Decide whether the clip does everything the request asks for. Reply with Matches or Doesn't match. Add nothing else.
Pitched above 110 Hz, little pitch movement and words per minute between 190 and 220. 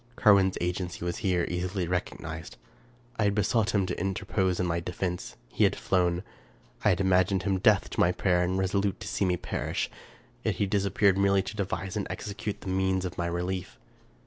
Doesn't match